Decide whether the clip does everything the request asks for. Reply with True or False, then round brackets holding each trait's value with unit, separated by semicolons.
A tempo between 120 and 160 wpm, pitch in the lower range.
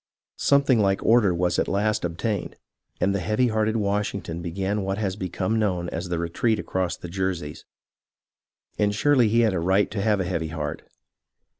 False (175 wpm; 100 Hz)